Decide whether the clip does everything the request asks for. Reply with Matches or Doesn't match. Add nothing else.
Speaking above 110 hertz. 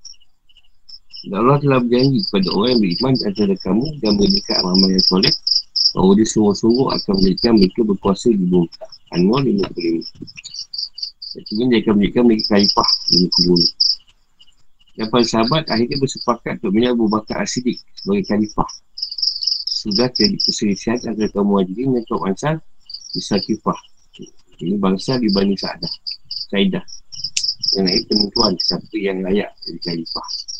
Doesn't match